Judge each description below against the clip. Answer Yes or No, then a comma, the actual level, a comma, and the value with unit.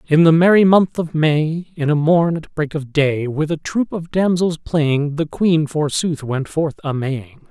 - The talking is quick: Yes, fast, 210 wpm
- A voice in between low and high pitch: Yes, medium, 155 Hz